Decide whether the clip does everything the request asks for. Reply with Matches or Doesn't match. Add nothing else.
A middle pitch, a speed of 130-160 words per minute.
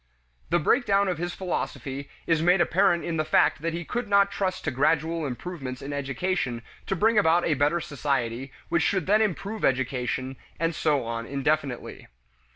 Doesn't match